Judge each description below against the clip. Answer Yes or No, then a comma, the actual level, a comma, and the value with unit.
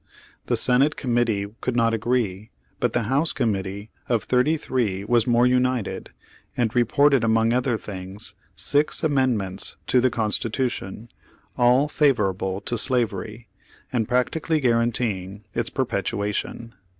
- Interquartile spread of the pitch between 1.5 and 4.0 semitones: Yes, average, 3.4 semitones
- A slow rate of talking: Yes, slow, 125 wpm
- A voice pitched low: Yes, low, 120 Hz